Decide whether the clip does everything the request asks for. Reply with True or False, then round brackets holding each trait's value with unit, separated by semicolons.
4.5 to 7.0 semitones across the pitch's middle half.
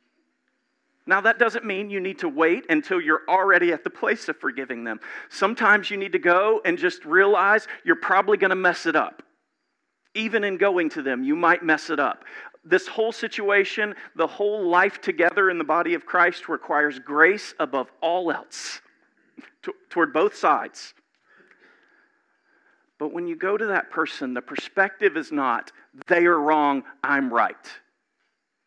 True (4.9 semitones)